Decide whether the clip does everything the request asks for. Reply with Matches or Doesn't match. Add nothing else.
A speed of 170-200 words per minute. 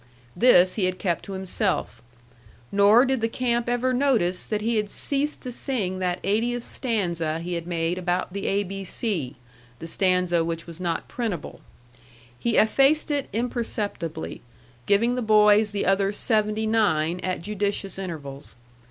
Doesn't match